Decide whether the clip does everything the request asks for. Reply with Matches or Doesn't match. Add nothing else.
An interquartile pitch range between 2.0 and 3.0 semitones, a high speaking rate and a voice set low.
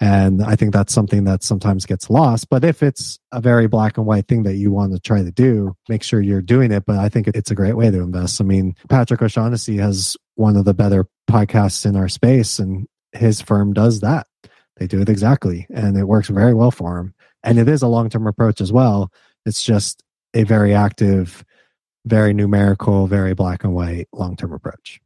Matches